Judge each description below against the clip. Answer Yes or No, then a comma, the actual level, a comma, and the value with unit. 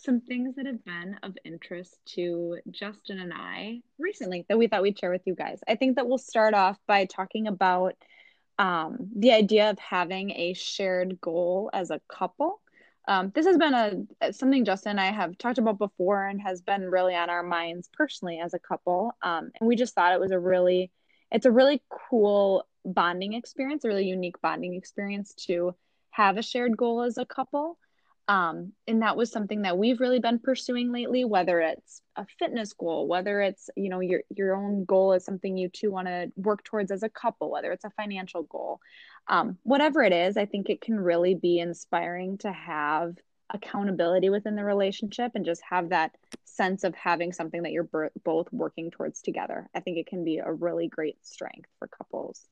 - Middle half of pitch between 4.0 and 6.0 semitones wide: Yes, average, 4.4 semitones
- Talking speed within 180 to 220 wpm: Yes, average, 200 wpm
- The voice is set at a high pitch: Yes, high, 195 Hz